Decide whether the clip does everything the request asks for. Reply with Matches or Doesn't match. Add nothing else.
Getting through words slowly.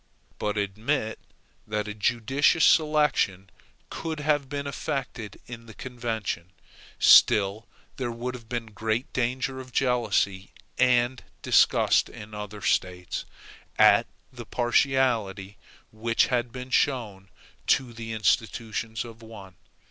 Matches